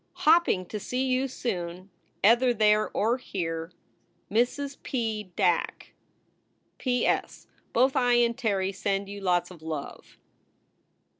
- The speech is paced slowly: Yes, slow, 125 wpm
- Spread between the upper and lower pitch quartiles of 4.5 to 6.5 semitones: Yes, average, 5.1 semitones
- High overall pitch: Yes, high, 215 Hz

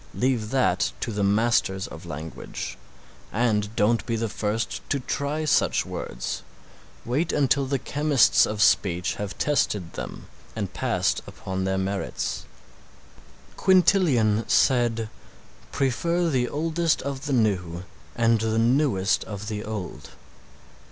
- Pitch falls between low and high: No, low, 115 Hz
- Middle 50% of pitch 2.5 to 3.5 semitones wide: No, average, 5.1 semitones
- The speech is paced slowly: Yes, slow, 125 wpm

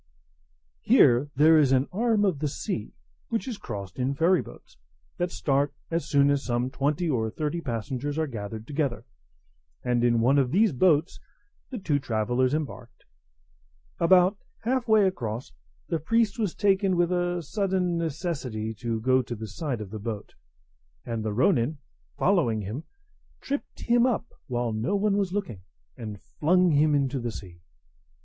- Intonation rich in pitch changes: Yes, wide, 7.2 semitones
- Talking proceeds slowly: No, average, 160 wpm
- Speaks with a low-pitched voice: No, medium, 145 Hz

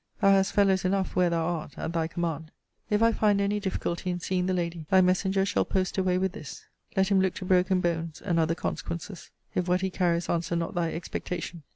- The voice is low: No, medium, 180 Hz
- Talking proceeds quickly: Yes, fast, 220 wpm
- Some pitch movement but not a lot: No, narrow, 2.0 semitones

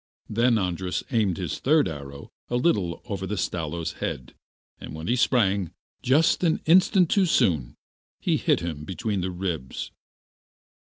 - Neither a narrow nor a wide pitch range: No, wide, 6.6 semitones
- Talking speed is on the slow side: No, average, 155 wpm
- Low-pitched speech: Yes, very low, 95 Hz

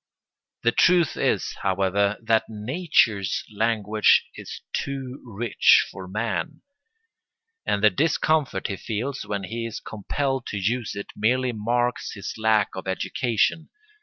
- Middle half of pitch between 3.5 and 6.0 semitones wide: Yes, average, 3.9 semitones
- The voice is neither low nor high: No, low, 110 Hz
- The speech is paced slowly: Yes, slow, 130 wpm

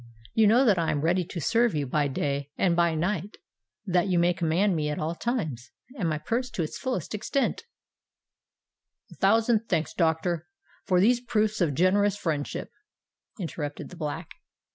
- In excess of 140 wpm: Yes, average, 165 wpm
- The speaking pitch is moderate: Yes, medium, 175 Hz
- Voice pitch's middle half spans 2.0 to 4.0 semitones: No, average, 5.2 semitones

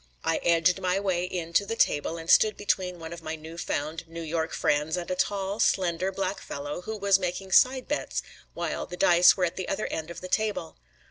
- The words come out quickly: Yes, fast, 220 wpm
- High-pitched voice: No, medium, 180 Hz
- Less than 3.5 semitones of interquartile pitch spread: Yes, average, 2.9 semitones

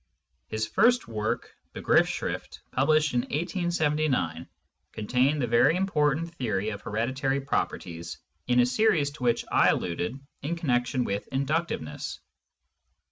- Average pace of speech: No, slow, 125 wpm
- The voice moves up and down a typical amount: No, wide, 5.7 semitones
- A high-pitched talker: No, low, 135 Hz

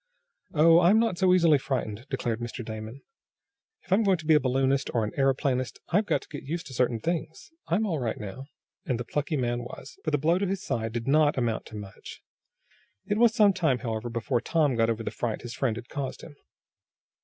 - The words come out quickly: Yes, fast, 220 wpm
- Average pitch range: No, wide, 5.8 semitones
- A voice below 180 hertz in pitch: Yes, low, 135 Hz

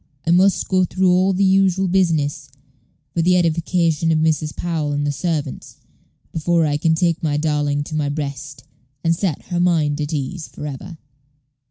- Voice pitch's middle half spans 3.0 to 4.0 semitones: Yes, average, 3.3 semitones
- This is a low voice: No, medium, 160 Hz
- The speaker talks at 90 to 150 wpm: No, average, 175 wpm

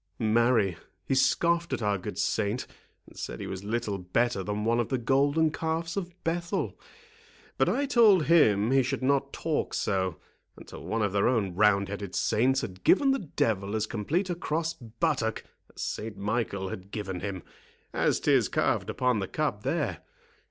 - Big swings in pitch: Yes, wide, 7.1 semitones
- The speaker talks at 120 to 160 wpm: No, average, 175 wpm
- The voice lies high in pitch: No, low, 115 Hz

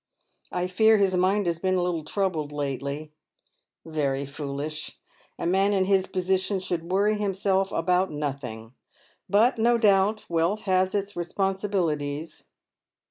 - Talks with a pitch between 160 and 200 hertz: Yes, medium, 185 Hz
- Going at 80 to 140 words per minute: Yes, slow, 135 wpm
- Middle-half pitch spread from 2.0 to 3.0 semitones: No, average, 4.4 semitones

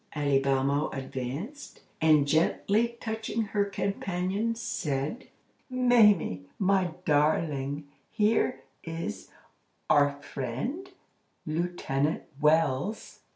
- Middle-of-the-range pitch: Yes, medium, 160 Hz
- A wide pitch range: Yes, wide, 6.8 semitones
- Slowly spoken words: Yes, slow, 75 wpm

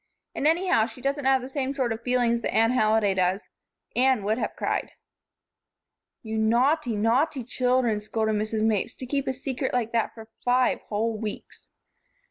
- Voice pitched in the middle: No, high, 235 Hz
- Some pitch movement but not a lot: Yes, average, 3.1 semitones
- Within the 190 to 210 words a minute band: No, average, 170 wpm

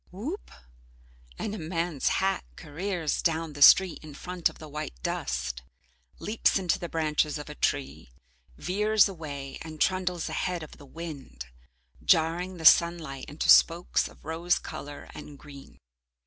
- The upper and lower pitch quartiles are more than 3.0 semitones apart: Yes, average, 3.6 semitones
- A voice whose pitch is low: No, medium, 160 Hz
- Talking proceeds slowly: No, average, 150 wpm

